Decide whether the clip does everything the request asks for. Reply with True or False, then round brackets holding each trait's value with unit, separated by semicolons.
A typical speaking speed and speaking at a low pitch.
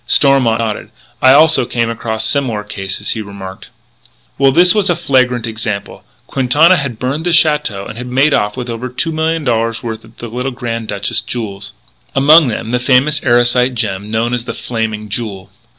True (180 wpm; 120 Hz)